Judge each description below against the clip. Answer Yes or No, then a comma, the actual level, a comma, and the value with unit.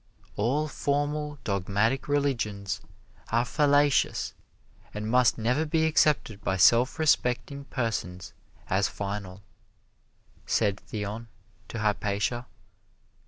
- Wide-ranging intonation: Yes, wide, 5.9 semitones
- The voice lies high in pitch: No, low, 115 Hz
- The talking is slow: Yes, slow, 95 wpm